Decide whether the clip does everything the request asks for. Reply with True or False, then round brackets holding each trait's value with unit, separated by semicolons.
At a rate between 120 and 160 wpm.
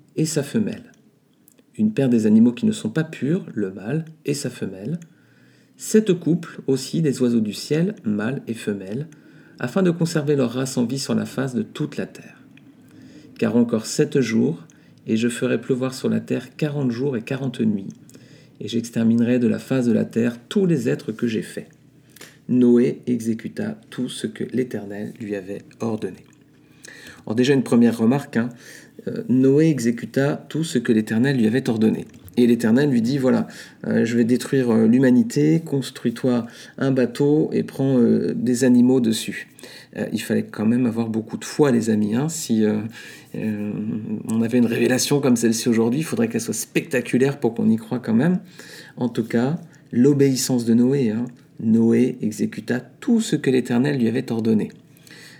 False (180 wpm)